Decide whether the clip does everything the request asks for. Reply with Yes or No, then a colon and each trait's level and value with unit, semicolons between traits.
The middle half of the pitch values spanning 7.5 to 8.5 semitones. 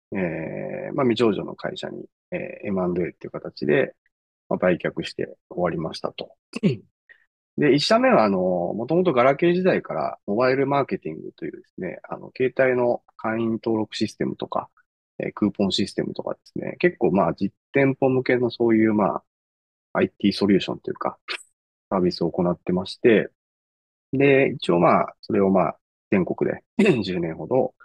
No: wide, 5.9 semitones